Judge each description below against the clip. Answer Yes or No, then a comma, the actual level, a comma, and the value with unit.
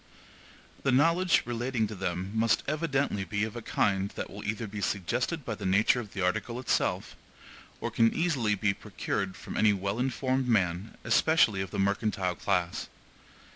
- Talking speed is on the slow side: No, average, 170 wpm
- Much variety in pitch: No, average, 4.3 semitones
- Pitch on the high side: No, low, 110 Hz